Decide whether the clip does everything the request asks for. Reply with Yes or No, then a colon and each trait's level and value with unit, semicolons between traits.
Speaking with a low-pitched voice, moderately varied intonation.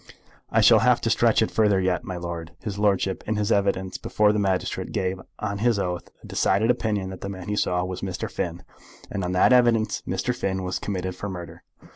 No: very low, 95 Hz; narrow, 2.3 semitones